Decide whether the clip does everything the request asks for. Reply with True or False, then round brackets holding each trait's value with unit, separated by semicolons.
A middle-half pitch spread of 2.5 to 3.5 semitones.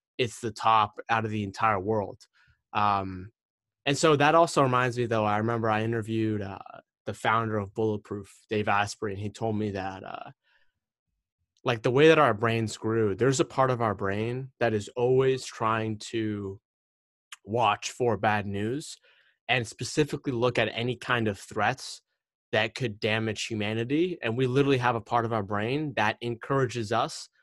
True (2.8 semitones)